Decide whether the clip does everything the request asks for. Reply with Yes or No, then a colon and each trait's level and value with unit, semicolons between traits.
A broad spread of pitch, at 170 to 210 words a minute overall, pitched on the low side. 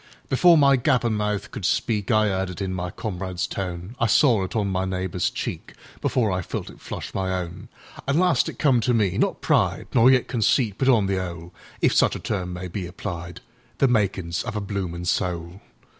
No: average, 4.3 semitones; average, 175 wpm; low, 100 Hz